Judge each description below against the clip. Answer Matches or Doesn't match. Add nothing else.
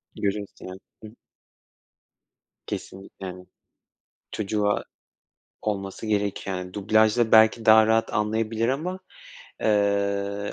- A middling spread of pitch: Doesn't match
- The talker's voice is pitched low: Matches